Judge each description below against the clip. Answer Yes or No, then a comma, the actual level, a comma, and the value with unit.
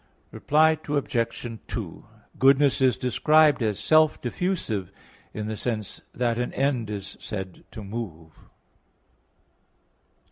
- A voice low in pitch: Yes, low, 120 Hz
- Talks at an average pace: No, slow, 110 wpm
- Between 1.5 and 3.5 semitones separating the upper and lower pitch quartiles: No, average, 5.2 semitones